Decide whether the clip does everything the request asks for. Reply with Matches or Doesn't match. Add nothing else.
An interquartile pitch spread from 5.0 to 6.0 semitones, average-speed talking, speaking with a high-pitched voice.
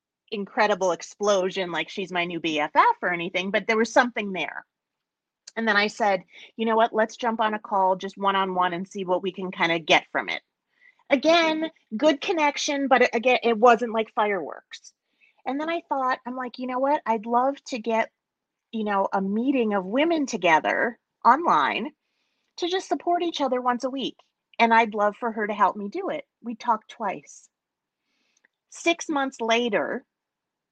Matches